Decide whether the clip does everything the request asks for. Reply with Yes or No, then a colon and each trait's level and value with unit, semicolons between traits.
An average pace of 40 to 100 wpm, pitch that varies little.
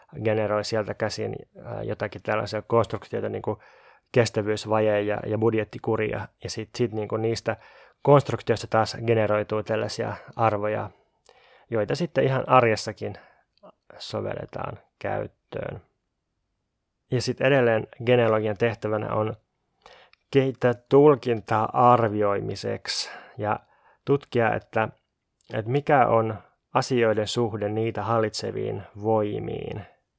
Yes: slow, 95 wpm; narrow, 2.1 semitones